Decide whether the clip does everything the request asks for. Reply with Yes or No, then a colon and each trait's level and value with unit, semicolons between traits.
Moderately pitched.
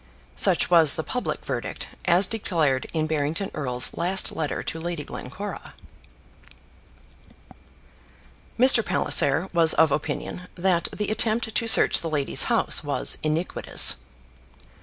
Yes: medium, 170 Hz